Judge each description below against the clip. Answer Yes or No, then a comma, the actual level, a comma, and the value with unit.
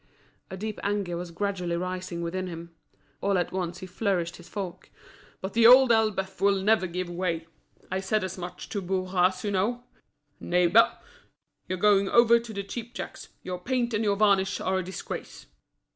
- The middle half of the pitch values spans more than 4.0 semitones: No, narrow, 2.6 semitones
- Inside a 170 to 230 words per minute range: Yes, average, 175 wpm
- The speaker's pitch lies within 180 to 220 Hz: Yes, high, 190 Hz